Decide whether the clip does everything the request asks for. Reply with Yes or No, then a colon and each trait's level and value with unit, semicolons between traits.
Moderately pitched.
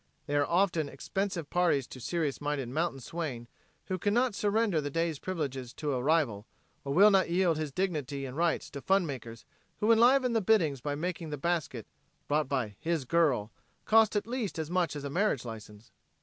Yes: medium, 160 Hz